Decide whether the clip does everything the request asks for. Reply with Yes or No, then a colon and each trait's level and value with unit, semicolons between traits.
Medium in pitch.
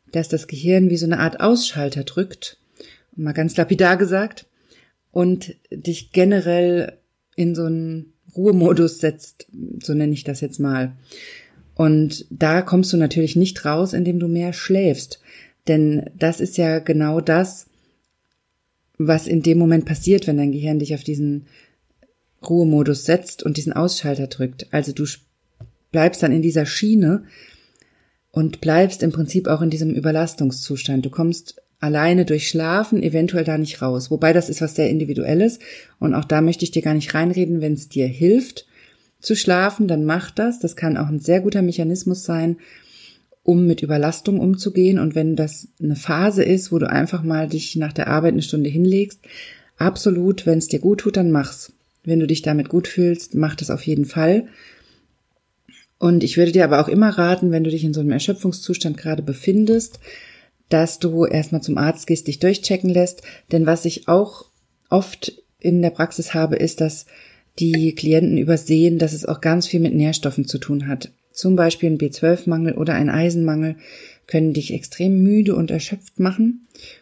Yes: medium, 165 Hz